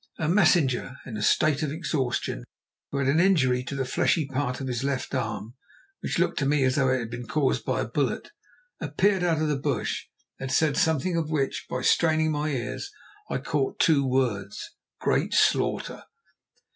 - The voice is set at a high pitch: No, medium, 140 Hz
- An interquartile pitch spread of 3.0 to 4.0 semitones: Yes, average, 3.5 semitones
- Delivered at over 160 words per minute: Yes, average, 185 wpm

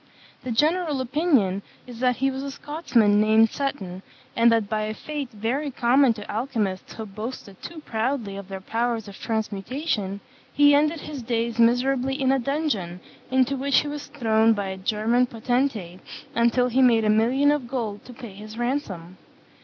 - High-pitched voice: Yes, high, 235 Hz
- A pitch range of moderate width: Yes, average, 4.1 semitones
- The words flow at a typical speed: Yes, average, 175 wpm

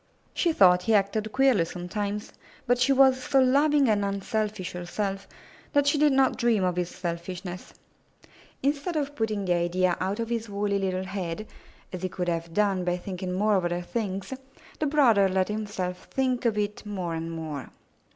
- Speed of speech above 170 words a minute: Yes, average, 180 wpm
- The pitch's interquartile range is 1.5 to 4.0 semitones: No, average, 4.6 semitones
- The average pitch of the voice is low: No, high, 200 Hz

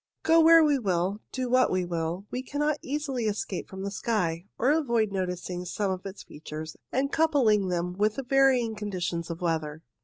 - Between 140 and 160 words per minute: No, average, 190 wpm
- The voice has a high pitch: Yes, high, 205 Hz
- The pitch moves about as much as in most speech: No, wide, 6.6 semitones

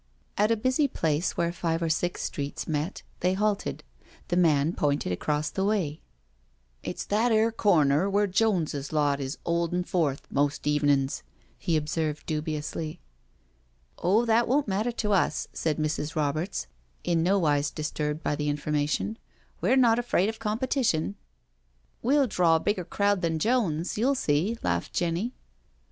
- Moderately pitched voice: Yes, medium, 165 Hz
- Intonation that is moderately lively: No, wide, 5.8 semitones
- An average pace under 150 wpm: No, average, 155 wpm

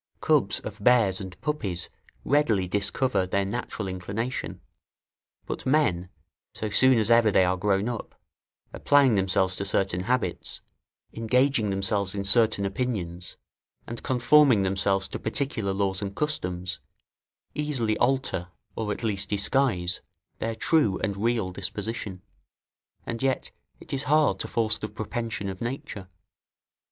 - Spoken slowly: Yes, slow, 130 wpm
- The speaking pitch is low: Yes, low, 105 Hz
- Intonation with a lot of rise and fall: No, average, 4.1 semitones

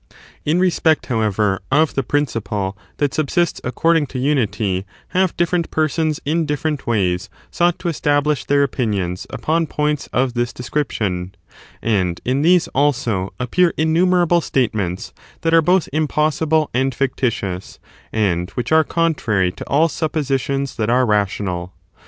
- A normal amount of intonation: No, wide, 6.7 semitones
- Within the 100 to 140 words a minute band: Yes, slow, 135 wpm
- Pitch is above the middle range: No, medium, 140 Hz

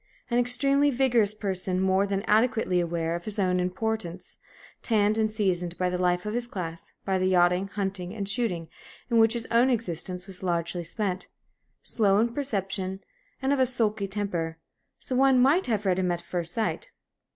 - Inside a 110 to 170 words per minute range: No, average, 180 wpm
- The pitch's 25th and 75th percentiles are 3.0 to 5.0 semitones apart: Yes, average, 4.2 semitones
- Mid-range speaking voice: No, high, 195 Hz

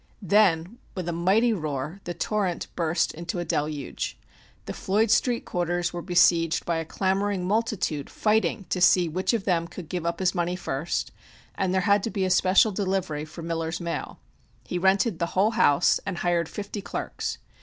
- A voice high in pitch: No, medium, 180 Hz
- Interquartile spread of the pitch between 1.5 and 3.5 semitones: Yes, average, 2.9 semitones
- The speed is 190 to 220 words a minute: No, average, 180 wpm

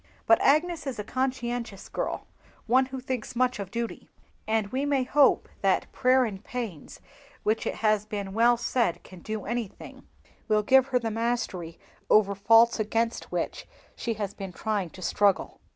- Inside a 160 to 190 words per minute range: Yes, average, 165 wpm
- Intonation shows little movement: No, average, 3.3 semitones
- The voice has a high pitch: Yes, high, 230 Hz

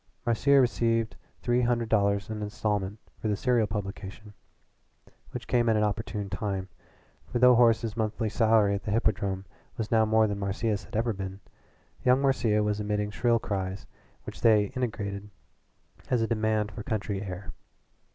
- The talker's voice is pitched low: Yes, low, 110 Hz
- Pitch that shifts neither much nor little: No, narrow, 2.2 semitones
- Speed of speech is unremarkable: Yes, average, 160 wpm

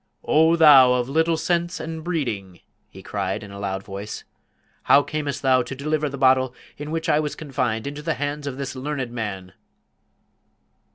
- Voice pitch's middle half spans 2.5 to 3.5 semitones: No, average, 3.9 semitones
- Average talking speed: Yes, average, 175 wpm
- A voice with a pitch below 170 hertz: Yes, medium, 140 Hz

